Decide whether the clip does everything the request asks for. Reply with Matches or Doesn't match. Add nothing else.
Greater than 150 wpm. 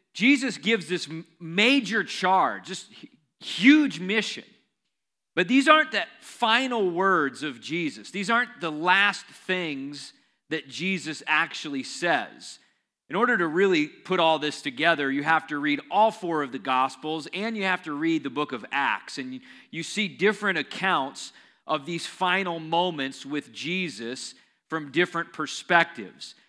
Doesn't match